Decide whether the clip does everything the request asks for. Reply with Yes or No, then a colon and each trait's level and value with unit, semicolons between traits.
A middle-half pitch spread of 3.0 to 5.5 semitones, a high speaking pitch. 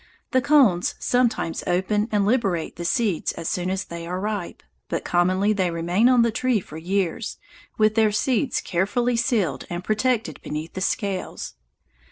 Yes: average, 4.7 semitones; high, 200 Hz